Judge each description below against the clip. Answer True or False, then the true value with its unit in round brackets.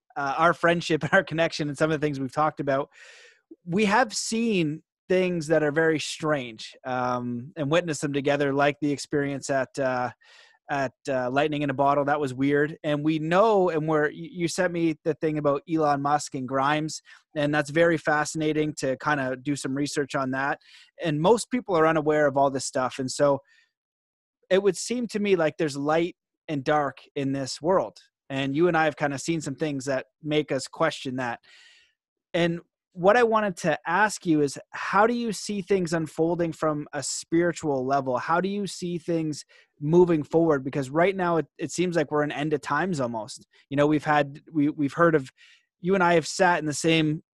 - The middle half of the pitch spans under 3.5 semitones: True (3.1 semitones)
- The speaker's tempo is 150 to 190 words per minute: False (205 wpm)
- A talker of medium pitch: True (155 Hz)